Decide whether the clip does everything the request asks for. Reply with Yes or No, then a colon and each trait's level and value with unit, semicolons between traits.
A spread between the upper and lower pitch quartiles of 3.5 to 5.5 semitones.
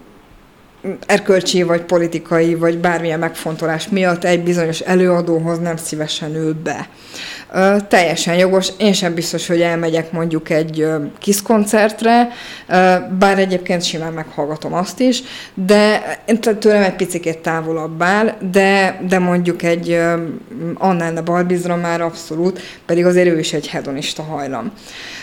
No: narrow, 2.5 semitones